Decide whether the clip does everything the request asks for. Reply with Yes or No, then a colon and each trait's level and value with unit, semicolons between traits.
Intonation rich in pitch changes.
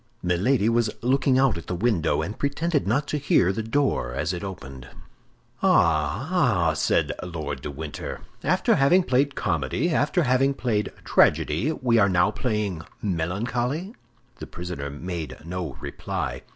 Yes: wide, 7.8 semitones